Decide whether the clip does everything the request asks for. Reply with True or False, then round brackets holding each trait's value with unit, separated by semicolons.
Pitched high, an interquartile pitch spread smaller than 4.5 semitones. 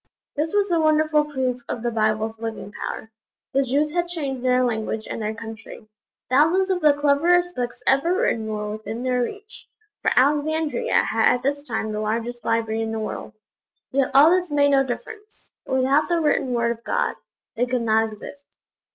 False (255 Hz; 5.1 semitones)